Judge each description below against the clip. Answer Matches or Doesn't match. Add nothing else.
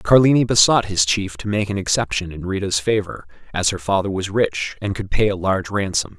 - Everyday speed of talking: Doesn't match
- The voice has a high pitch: Doesn't match